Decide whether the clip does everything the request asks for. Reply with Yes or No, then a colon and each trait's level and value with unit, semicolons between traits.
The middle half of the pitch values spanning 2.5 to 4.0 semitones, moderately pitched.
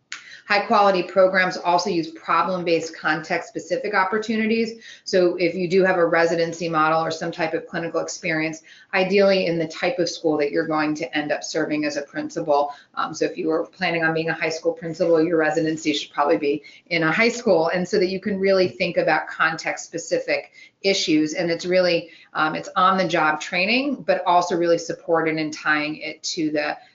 Yes: average, 2.8 semitones; medium, 170 Hz